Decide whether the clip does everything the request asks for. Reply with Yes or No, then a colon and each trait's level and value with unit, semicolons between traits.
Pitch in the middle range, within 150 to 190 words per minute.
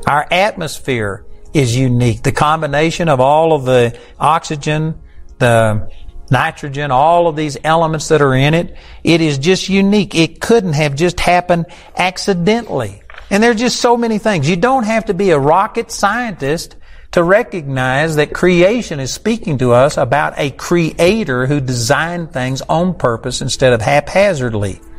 Yes: medium, 155 Hz; average, 155 wpm